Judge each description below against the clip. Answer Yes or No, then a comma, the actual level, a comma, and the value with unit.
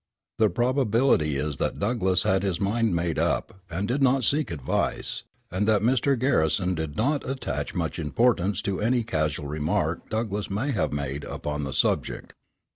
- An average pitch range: No, wide, 7.2 semitones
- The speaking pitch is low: Yes, low, 100 Hz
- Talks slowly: No, average, 165 wpm